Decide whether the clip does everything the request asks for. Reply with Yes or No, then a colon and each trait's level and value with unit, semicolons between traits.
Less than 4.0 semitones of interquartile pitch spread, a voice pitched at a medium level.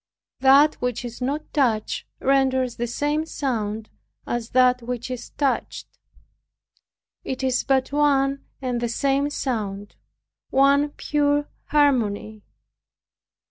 No: average, 2.9 semitones; very high, 260 Hz